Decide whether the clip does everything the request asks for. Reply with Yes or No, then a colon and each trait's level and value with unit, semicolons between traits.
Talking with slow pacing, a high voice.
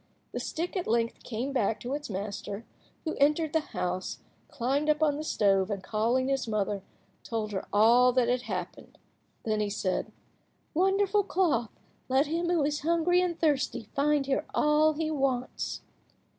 No: average, 165 wpm; very high, 270 Hz